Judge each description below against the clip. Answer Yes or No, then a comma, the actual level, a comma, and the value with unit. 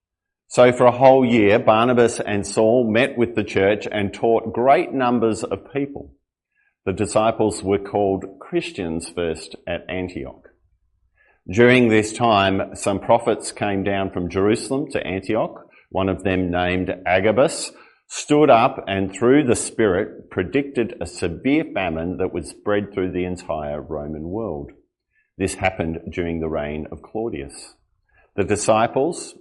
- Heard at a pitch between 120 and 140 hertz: No, low, 100 Hz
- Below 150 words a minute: Yes, average, 140 wpm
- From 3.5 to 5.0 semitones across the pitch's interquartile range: Yes, average, 4.4 semitones